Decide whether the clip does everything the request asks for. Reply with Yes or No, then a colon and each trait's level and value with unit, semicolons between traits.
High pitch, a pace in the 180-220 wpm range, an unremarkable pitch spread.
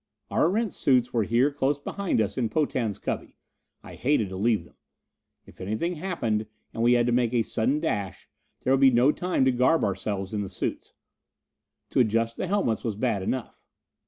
No: low, 120 Hz; average, 190 wpm; average, 4.6 semitones